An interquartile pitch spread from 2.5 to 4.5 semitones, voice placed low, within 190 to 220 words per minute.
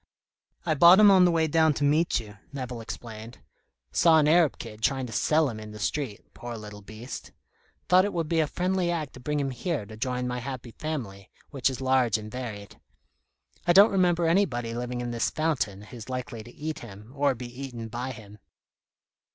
No: wide, 5.6 semitones; low, 130 Hz; average, 200 wpm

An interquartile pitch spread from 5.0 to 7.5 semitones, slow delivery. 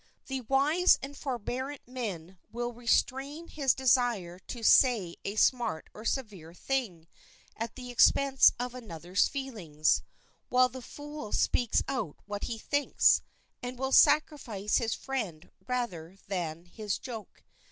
Yes: average, 5.3 semitones; slow, 130 wpm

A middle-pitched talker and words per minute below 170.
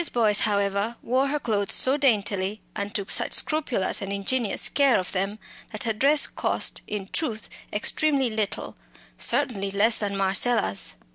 No: high, 215 Hz; average, 150 wpm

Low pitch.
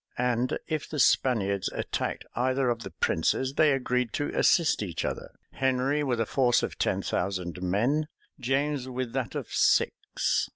Yes: low, 125 Hz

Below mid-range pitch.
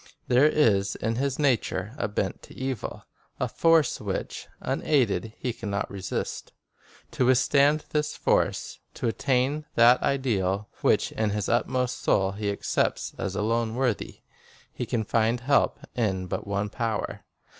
Yes: low, 115 Hz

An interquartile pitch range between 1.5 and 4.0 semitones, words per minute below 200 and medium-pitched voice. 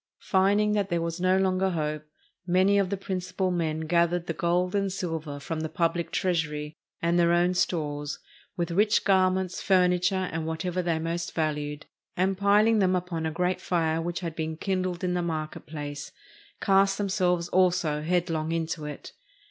Yes: narrow, 2.6 semitones; average, 170 wpm; medium, 175 Hz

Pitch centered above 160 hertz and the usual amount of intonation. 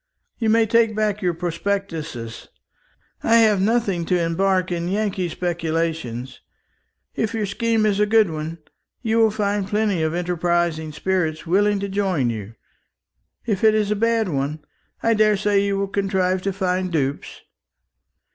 Yes: high, 190 Hz; average, 4.0 semitones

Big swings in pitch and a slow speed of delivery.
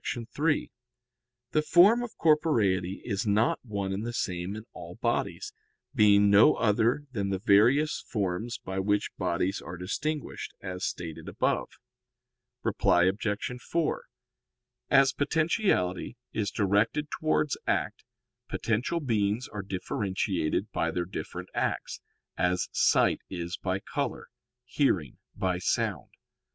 Yes: wide, 6.0 semitones; slow, 120 wpm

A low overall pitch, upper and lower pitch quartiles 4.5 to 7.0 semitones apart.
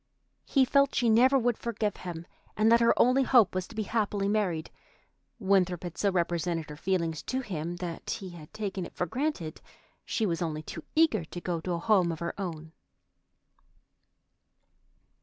No: medium, 185 Hz; average, 4.9 semitones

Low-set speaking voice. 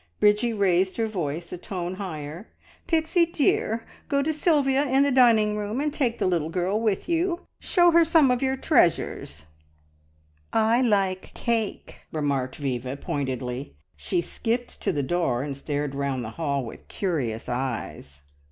No: high, 190 Hz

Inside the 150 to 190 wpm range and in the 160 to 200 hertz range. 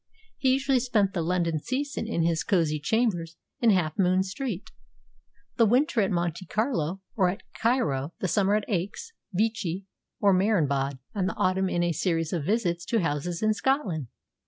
Yes: average, 170 wpm; high, 190 Hz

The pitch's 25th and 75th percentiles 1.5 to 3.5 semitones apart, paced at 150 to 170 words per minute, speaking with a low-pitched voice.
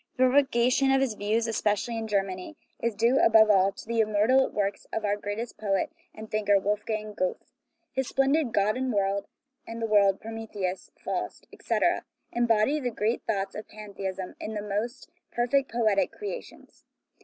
No: average, 2.8 semitones; average, 160 wpm; high, 215 Hz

